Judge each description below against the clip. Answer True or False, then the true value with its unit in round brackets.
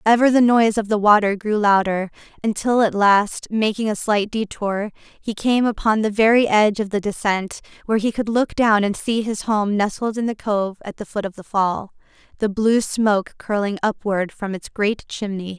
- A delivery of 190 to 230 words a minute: True (200 wpm)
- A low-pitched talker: False (210 Hz)